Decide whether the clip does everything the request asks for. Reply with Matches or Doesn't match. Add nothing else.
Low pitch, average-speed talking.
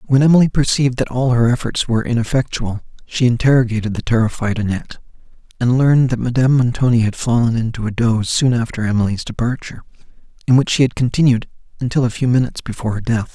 Matches